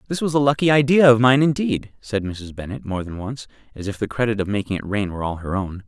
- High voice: No, low, 115 Hz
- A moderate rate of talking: No, fast, 265 wpm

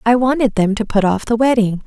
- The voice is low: No, high, 225 Hz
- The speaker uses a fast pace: Yes, fast, 255 wpm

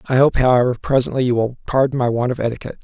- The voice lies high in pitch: No, low, 125 Hz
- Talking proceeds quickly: Yes, fast, 235 wpm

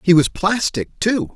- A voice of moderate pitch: Yes, medium, 180 Hz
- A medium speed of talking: Yes, average, 180 wpm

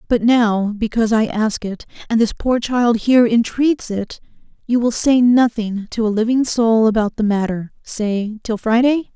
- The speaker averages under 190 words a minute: Yes, average, 175 wpm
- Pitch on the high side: Yes, high, 225 Hz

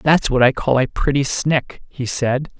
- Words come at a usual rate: No, fast, 210 wpm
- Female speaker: No, male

